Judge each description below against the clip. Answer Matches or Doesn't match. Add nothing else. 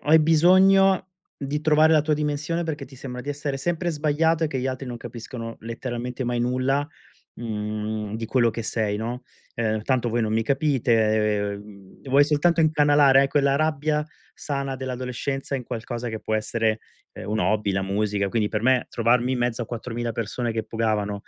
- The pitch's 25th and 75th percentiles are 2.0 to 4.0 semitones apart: Doesn't match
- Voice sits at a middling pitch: Doesn't match